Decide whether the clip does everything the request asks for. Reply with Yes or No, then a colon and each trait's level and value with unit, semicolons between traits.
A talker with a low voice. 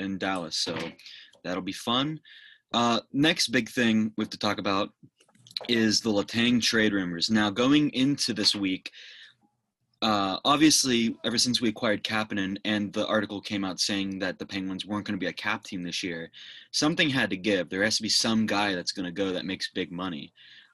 Yes: low, 105 Hz